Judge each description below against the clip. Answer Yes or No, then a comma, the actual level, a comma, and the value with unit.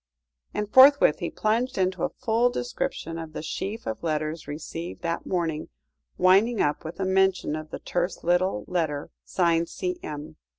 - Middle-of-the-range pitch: Yes, medium, 175 Hz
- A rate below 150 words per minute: No, average, 160 wpm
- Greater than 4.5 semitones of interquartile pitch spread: No, average, 4.1 semitones